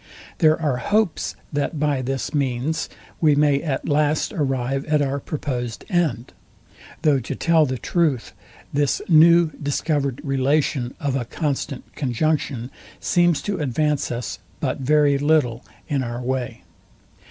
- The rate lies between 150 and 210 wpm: No, slow, 135 wpm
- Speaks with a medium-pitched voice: Yes, medium, 145 Hz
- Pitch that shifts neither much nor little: Yes, average, 3.0 semitones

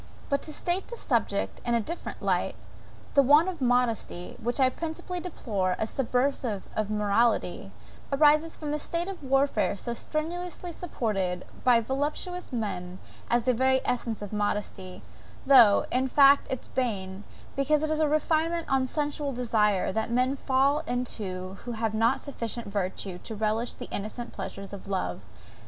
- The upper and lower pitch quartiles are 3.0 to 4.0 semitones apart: No, wide, 5.6 semitones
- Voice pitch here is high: Yes, high, 245 Hz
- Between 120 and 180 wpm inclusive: Yes, average, 160 wpm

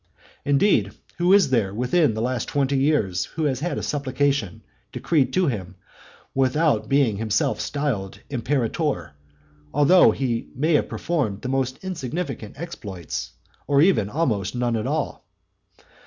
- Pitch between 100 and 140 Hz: Yes, low, 135 Hz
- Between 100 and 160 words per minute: Yes, average, 140 wpm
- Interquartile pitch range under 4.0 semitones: No, average, 5.2 semitones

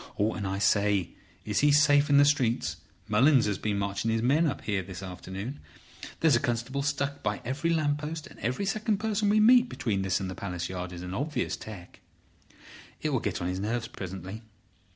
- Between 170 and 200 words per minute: Yes, average, 195 wpm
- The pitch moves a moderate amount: No, wide, 6.9 semitones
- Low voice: Yes, low, 115 Hz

